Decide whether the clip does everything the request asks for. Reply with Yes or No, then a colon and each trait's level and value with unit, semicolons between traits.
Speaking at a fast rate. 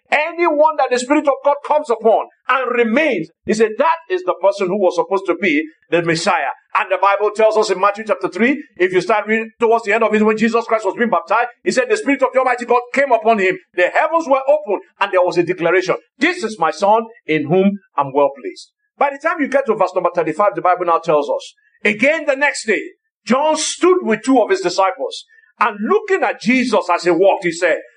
Yes: fast, 235 wpm